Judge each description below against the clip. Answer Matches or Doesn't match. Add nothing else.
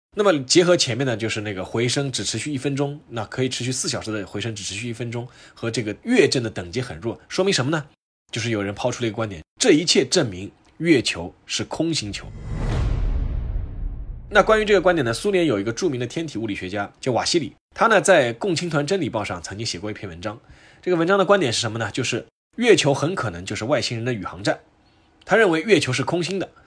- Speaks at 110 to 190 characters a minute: Doesn't match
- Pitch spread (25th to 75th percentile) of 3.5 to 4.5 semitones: Doesn't match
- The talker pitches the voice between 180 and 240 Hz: Doesn't match